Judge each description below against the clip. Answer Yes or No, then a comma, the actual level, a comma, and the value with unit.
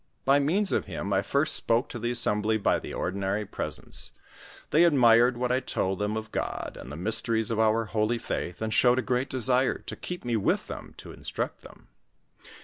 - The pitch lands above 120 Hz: No, low, 115 Hz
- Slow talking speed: No, average, 200 wpm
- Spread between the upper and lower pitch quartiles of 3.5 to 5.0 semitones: No, average, 3.1 semitones